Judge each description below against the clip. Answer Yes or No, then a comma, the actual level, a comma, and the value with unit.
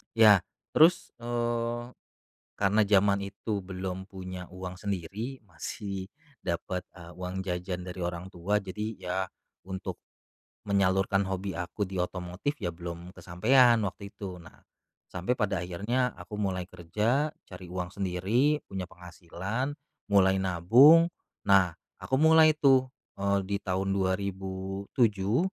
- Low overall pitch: Yes, very low, 95 Hz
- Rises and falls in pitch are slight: No, average, 3.1 semitones